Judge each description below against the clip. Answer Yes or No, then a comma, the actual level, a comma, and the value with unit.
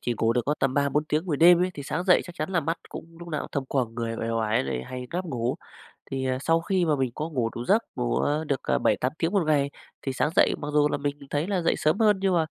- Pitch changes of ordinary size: Yes, average, 4.7 semitones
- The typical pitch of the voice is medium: Yes, medium, 150 Hz